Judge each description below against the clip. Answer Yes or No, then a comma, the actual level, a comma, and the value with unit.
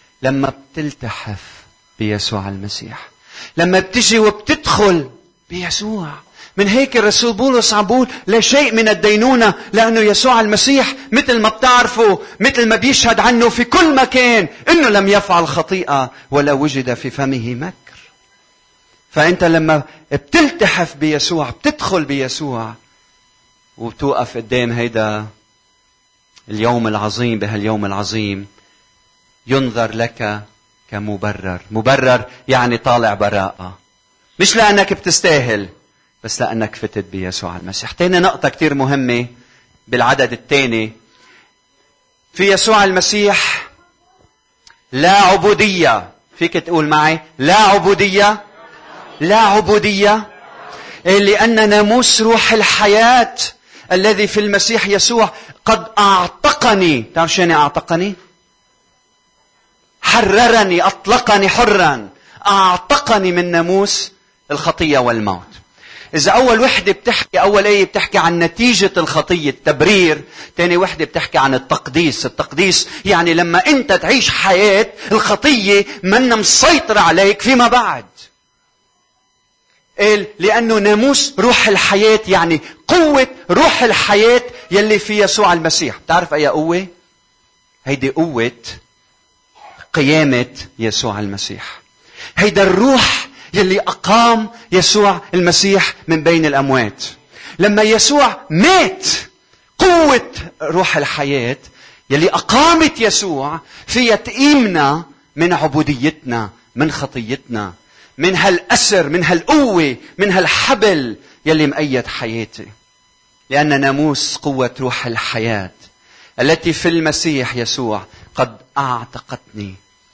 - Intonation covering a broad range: Yes, wide, 8.6 semitones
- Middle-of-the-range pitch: Yes, medium, 175 Hz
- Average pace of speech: Yes, average, 100 wpm